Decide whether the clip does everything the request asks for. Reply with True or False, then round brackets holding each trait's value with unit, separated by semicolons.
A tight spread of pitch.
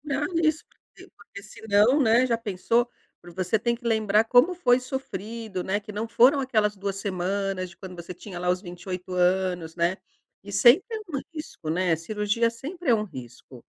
False (4.7 semitones)